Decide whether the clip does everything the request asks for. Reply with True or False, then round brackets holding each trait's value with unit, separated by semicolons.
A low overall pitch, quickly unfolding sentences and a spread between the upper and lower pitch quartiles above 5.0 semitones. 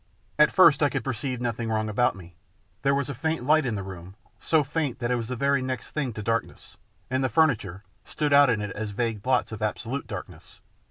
False (125 Hz; 225 wpm; 4.4 semitones)